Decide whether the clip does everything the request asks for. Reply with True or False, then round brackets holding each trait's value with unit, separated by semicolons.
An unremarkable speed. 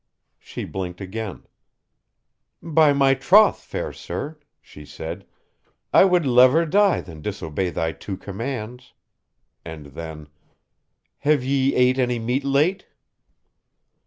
False (115 wpm)